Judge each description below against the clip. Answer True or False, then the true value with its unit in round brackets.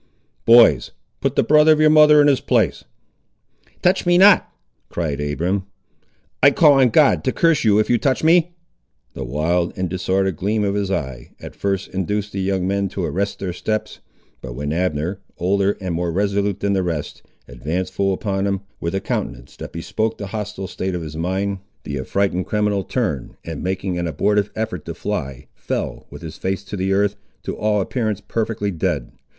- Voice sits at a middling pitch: False (95 Hz)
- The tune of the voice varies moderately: True (3.4 semitones)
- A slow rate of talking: False (190 wpm)